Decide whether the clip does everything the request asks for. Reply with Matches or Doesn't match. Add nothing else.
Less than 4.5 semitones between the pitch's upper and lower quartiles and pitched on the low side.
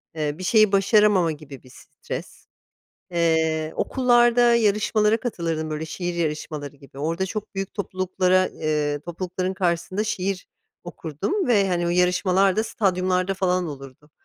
Doesn't match